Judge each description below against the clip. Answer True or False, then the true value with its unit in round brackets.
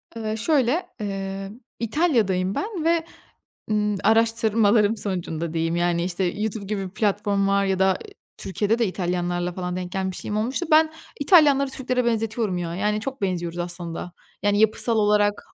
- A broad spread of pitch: False (3.7 semitones)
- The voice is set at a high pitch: True (205 Hz)